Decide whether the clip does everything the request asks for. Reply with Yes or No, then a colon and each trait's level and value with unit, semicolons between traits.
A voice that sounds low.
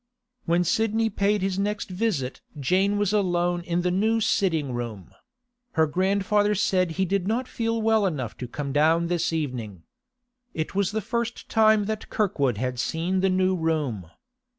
No: medium, 185 Hz